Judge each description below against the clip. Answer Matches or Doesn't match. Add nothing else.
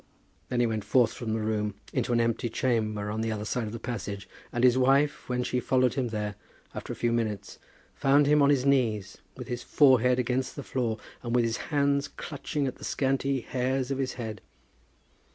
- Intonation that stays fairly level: Doesn't match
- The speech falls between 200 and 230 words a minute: Matches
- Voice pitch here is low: Matches